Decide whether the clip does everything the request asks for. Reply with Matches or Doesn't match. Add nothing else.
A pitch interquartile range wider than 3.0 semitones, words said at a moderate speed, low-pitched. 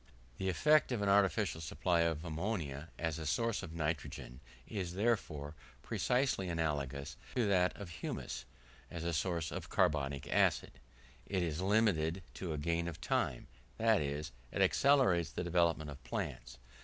Matches